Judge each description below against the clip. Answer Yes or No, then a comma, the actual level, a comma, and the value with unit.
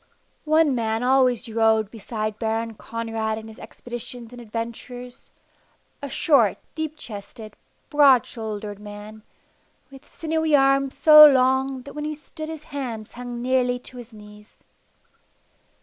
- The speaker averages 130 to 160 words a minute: Yes, slow, 135 wpm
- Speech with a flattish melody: No, average, 3.7 semitones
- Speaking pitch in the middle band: No, high, 245 Hz